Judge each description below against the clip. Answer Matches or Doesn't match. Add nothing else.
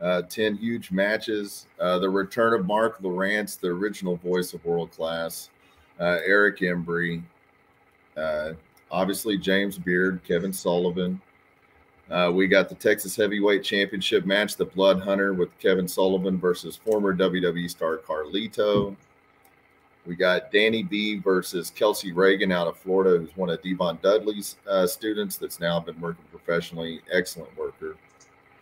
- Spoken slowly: Doesn't match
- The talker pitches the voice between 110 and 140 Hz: Doesn't match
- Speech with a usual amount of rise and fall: Doesn't match